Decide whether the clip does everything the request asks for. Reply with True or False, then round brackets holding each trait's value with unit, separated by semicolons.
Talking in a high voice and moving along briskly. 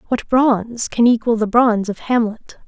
False (230 Hz; 180 wpm)